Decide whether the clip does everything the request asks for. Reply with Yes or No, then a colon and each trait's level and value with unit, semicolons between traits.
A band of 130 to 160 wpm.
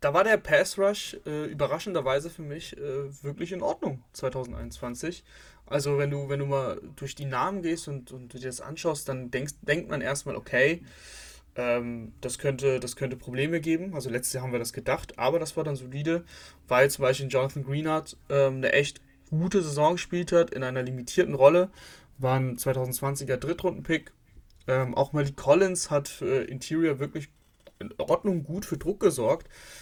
No: average, 180 wpm